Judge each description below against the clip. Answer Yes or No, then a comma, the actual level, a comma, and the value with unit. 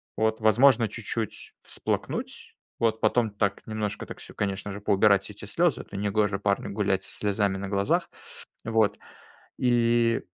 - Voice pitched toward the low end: Yes, low, 105 Hz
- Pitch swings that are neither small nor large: No, narrow, 2.1 semitones